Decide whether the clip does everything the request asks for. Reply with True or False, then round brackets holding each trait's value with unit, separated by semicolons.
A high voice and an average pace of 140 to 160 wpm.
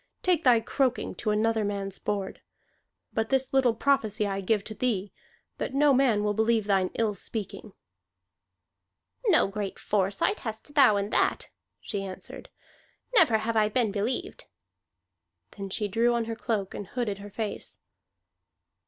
True (220 Hz; 150 wpm)